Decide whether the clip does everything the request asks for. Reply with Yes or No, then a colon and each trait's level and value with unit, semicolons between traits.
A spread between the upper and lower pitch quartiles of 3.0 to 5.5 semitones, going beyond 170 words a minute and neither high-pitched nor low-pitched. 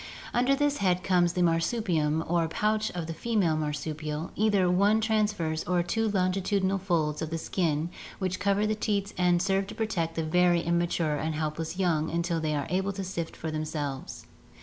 Yes: average, 3.8 semitones; average, 185 wpm; medium, 175 Hz